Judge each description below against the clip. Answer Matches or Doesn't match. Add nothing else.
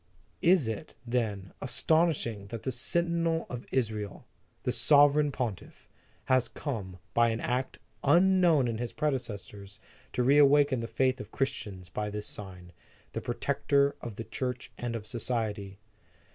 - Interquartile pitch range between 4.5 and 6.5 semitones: Matches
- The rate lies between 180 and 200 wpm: Doesn't match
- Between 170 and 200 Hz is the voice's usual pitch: Doesn't match